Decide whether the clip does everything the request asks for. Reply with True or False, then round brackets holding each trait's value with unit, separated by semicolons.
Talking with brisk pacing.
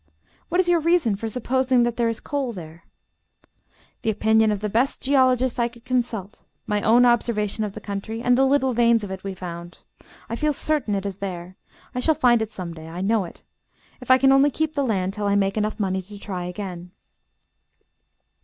True (210 wpm)